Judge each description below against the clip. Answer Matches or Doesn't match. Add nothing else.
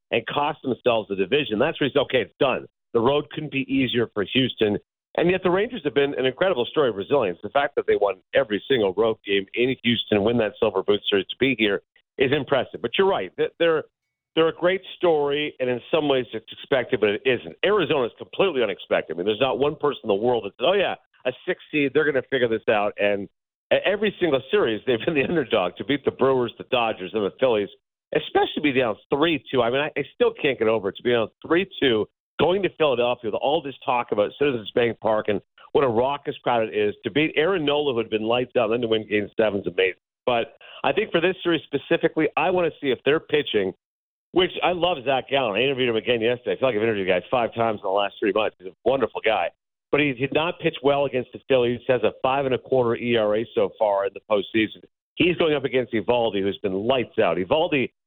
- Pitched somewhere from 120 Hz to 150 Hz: Matches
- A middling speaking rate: Doesn't match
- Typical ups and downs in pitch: Doesn't match